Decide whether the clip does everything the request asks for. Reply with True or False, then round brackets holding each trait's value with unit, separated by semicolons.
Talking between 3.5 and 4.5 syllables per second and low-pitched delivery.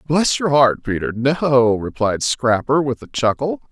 True (4.2 syllables/s; 130 Hz)